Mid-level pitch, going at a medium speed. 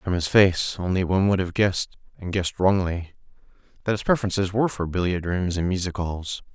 No: very low, 90 Hz; average, 190 wpm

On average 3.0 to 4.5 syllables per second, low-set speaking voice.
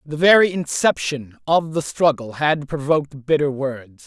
No: 4.4 syllables/s; medium, 145 Hz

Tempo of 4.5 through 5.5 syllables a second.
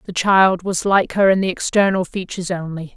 Yes: 5.3 syllables/s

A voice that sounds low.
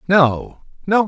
No: medium, 175 Hz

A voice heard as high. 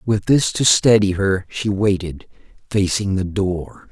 No: low, 100 Hz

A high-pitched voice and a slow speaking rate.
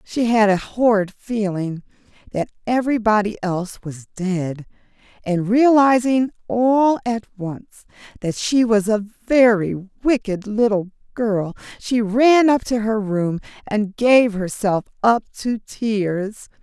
Yes: high, 215 Hz; slow, 125 wpm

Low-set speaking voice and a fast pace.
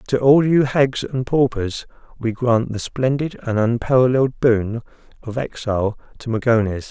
No: low, 120 Hz; average, 150 wpm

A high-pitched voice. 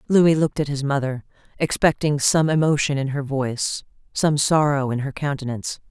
No: medium, 140 Hz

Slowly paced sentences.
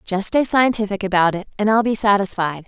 No: average, 200 wpm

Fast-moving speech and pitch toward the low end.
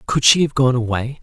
Yes: fast, 245 wpm; low, 130 Hz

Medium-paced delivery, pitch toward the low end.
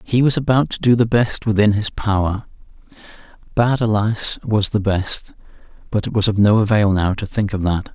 Yes: average, 195 wpm; low, 105 Hz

